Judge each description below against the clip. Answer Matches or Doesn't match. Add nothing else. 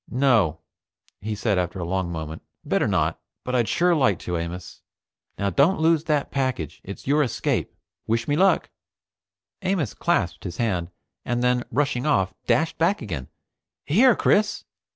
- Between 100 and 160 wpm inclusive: Matches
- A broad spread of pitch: Matches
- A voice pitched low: Matches